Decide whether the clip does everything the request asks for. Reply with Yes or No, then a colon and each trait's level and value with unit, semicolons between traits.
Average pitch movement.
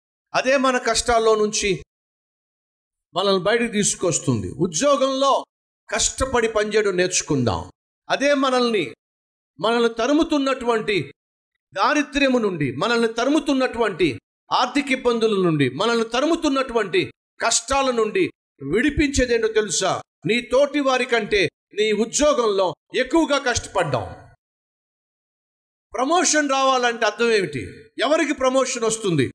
Yes: average, 4.5 semitones